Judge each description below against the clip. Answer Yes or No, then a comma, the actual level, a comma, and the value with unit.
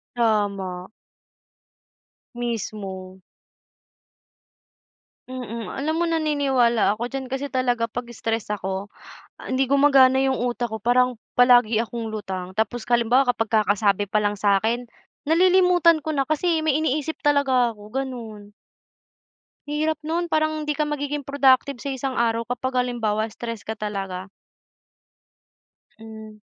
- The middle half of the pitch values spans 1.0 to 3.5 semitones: No, average, 4.5 semitones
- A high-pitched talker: Yes, high, 245 Hz